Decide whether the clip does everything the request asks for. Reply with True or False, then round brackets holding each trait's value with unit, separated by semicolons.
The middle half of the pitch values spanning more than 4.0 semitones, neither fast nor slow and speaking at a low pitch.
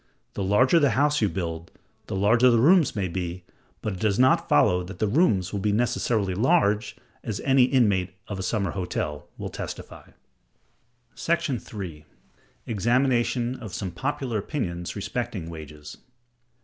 True (5.2 semitones; 150 wpm; 105 Hz)